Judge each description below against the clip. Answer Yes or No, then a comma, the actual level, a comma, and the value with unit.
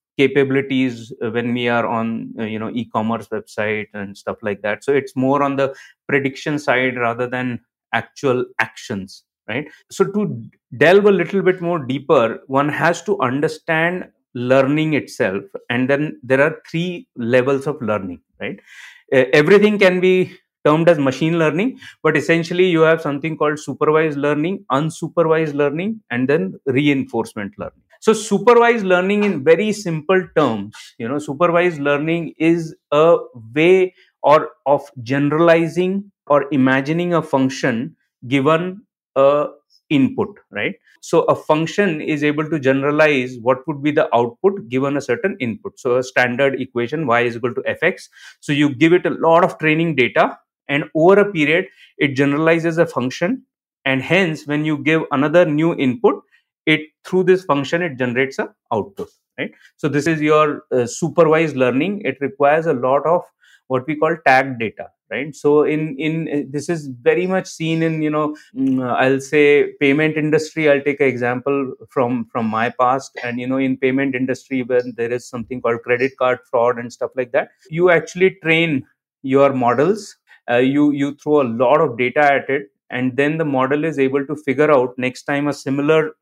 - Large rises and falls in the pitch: No, average, 4.0 semitones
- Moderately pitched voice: Yes, medium, 145 Hz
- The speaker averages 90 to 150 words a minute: No, average, 170 wpm